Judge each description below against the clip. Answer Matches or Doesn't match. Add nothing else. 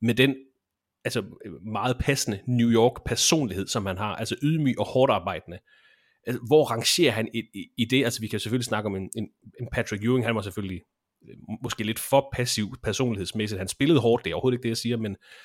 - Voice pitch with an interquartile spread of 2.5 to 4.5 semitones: Matches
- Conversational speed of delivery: Matches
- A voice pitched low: Matches